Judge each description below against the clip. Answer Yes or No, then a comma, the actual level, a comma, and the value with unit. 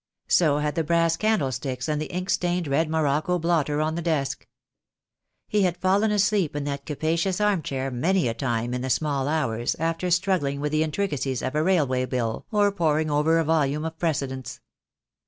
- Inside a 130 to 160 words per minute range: No, average, 185 wpm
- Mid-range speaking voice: Yes, medium, 155 Hz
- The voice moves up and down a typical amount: Yes, average, 4.0 semitones